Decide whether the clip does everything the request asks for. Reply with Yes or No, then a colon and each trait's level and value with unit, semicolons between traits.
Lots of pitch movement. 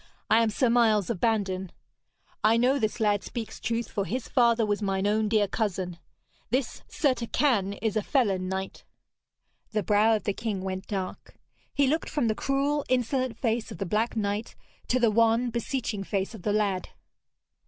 No: average, 2.9 semitones